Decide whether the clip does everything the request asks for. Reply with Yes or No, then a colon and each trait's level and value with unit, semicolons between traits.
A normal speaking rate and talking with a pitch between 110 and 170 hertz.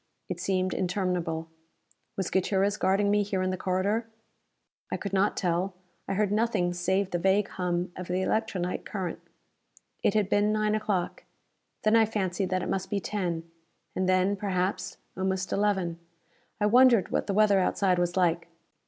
No: average, 165 wpm; high, 190 Hz